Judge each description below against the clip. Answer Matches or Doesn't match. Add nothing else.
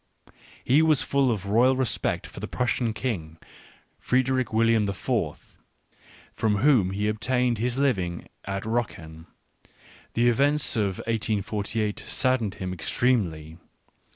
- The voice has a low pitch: Matches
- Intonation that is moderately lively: Matches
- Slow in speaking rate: Matches